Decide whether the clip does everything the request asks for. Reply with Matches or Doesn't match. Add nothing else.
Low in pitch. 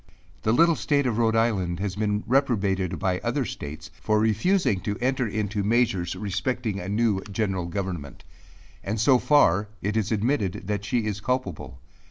Matches